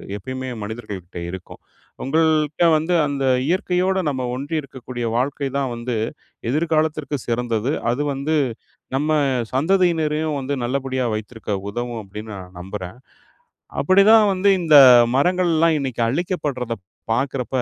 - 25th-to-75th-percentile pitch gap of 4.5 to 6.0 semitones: Yes, average, 4.8 semitones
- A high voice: No, low, 135 Hz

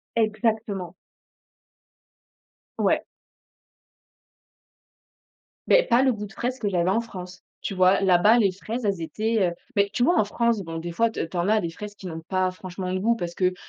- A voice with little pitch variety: No, average, 3.6 semitones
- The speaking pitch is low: No, high, 200 Hz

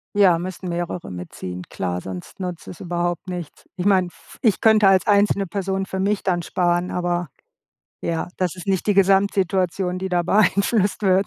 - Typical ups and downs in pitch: No, narrow, 2.0 semitones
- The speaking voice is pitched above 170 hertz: Yes, medium, 185 Hz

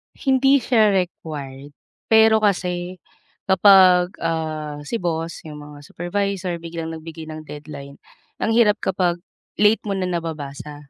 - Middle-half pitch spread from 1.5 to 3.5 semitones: No, average, 4.4 semitones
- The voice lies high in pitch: No, medium, 175 Hz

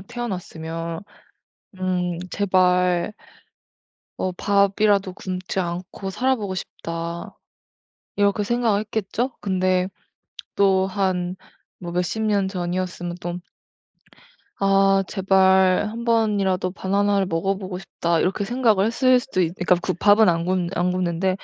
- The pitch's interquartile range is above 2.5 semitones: No, narrow, 2.1 semitones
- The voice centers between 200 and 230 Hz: No, high, 190 Hz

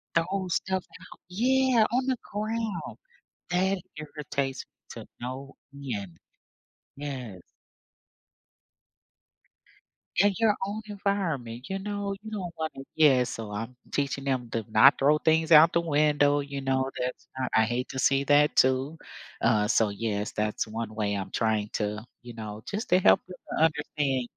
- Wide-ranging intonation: Yes, wide, 7.4 semitones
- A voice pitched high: No, medium, 140 Hz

